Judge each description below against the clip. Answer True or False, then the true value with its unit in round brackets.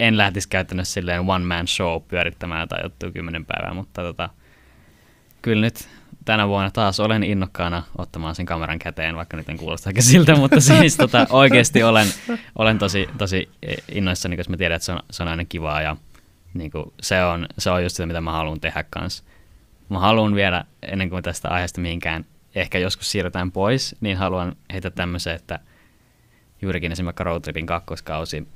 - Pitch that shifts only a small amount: False (3.1 semitones)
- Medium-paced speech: False (175 wpm)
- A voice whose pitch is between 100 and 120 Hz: False (90 Hz)